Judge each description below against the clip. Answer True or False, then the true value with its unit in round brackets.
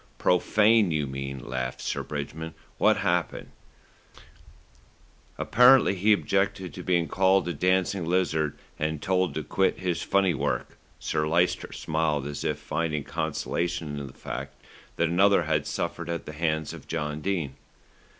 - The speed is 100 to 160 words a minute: True (145 wpm)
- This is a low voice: True (85 Hz)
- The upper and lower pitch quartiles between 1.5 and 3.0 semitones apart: False (3.8 semitones)